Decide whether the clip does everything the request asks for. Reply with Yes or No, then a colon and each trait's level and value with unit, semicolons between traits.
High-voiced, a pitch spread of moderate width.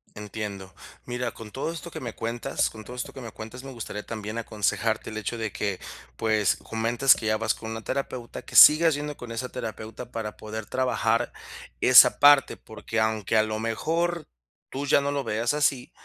No: low, 115 Hz; average, 3.1 semitones